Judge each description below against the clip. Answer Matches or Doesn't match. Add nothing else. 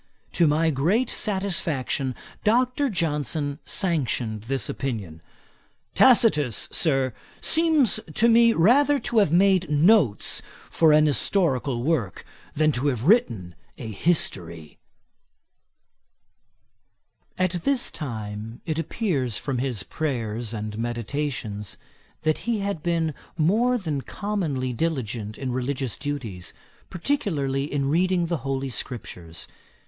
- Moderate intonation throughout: Doesn't match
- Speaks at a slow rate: Matches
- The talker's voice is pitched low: Doesn't match